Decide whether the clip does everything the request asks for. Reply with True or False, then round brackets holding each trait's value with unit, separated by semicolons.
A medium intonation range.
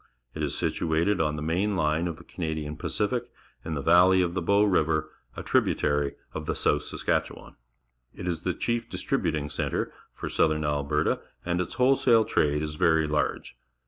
True (3.1 semitones)